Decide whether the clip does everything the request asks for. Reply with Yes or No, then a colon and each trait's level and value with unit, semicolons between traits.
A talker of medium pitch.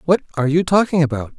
Yes: medium, 155 Hz